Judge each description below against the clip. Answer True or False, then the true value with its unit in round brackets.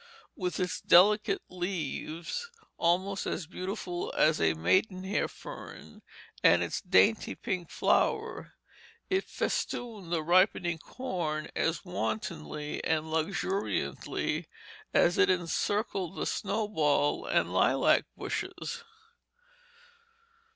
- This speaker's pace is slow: True (95 wpm)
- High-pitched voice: False (180 Hz)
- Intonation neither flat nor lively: True (3.8 semitones)